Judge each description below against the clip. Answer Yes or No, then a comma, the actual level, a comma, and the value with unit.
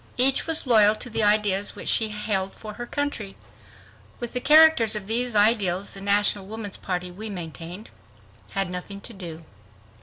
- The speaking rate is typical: Yes, average, 175 wpm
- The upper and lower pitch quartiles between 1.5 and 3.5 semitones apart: Yes, average, 2.9 semitones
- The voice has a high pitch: Yes, high, 210 Hz